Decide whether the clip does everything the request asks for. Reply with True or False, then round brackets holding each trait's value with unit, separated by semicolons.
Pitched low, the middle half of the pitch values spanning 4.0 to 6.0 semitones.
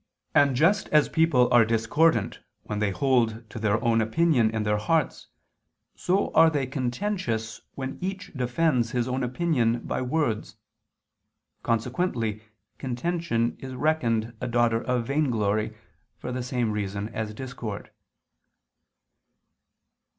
True (125 Hz; 4.6 semitones)